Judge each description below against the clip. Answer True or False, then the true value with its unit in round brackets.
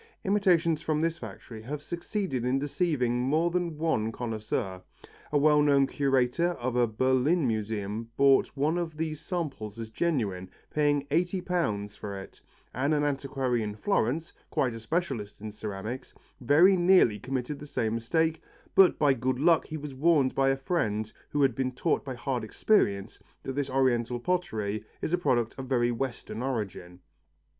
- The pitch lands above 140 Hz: False (135 Hz)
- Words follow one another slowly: False (165 wpm)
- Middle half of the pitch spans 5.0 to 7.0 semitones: True (5.5 semitones)